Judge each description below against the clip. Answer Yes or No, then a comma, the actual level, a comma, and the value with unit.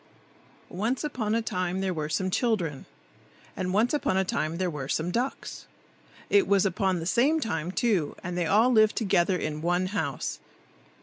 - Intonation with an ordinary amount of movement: Yes, average, 4.3 semitones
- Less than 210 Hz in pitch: Yes, medium, 185 Hz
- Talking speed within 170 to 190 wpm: Yes, average, 175 wpm